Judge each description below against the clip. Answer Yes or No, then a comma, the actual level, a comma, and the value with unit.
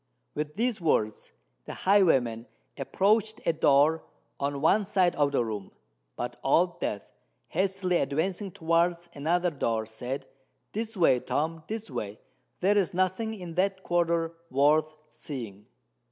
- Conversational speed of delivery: No, slow, 125 wpm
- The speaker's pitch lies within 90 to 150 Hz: No, medium, 165 Hz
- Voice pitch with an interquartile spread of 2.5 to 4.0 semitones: No, average, 5.2 semitones